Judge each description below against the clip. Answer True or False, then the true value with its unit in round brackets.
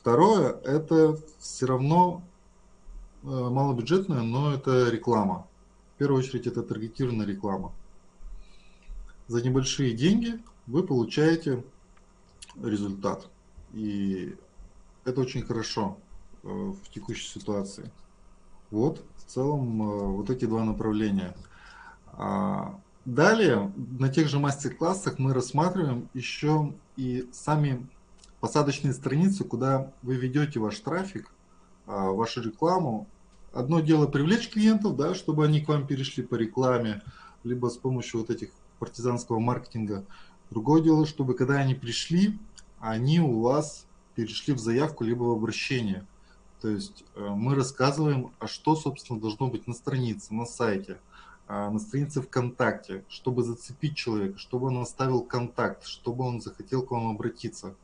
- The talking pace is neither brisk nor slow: True (120 wpm)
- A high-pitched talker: False (125 Hz)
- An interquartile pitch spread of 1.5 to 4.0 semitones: False (4.5 semitones)